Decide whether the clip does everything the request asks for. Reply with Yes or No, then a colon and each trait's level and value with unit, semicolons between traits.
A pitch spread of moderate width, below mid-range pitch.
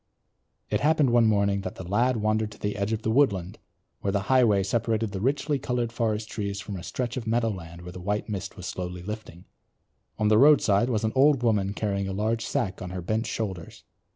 Yes: average, 3.0 semitones; low, 105 Hz